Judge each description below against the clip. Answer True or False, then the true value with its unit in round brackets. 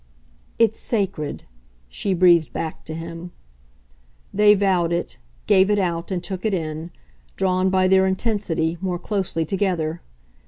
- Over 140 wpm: False (135 wpm)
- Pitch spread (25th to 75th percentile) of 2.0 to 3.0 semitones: True (2.6 semitones)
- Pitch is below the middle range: False (185 Hz)